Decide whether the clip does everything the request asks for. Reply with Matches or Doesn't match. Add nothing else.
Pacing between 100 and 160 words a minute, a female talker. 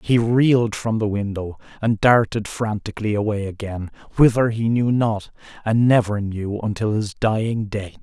Doesn't match